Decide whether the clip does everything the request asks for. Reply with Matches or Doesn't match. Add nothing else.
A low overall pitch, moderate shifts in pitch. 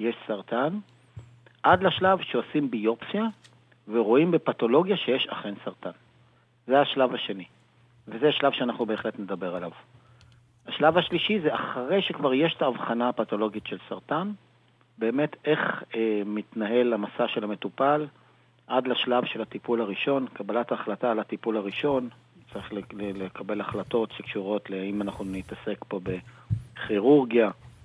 Matches